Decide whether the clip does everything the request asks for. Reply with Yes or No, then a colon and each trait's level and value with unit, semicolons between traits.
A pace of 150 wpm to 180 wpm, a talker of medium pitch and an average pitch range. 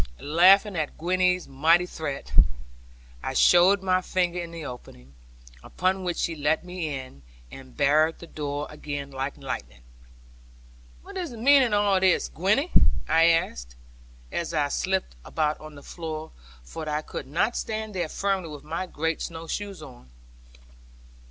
Yes: average, 155 wpm; medium, 165 Hz; average, 4.0 semitones